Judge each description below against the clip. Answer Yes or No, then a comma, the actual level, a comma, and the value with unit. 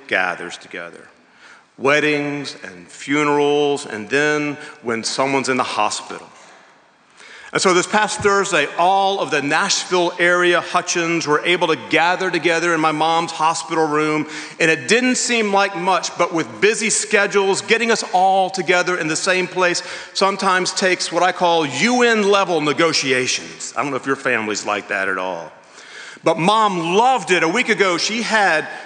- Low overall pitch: No, medium, 175 Hz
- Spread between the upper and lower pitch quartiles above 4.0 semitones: Yes, average, 4.5 semitones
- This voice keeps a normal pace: Yes, average, 160 wpm